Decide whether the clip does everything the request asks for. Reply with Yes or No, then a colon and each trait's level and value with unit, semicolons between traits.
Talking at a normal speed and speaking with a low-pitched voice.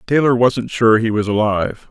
Yes: average, 190 wpm; low, 115 Hz